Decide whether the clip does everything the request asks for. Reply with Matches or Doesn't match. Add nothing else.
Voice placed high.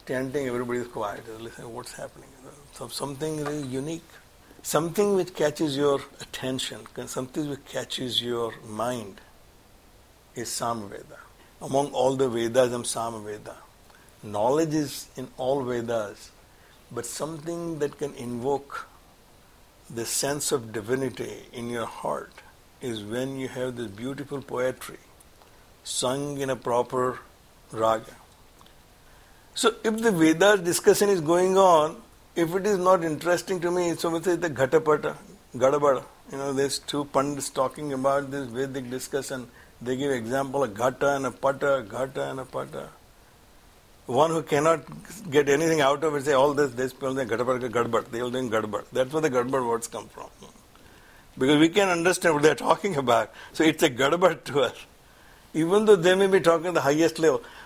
Doesn't match